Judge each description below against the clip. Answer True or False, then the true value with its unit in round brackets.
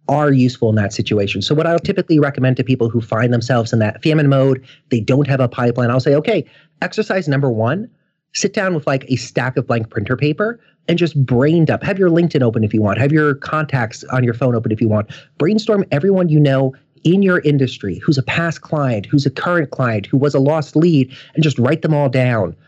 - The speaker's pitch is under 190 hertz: True (140 Hz)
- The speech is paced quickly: True (230 wpm)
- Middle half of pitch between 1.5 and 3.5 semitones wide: False (4.3 semitones)